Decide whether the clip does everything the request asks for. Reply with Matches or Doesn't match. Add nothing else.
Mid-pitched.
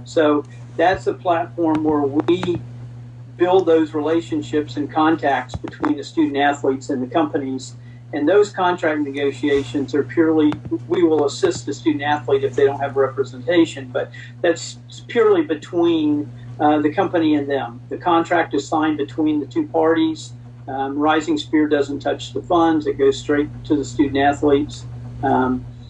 Matches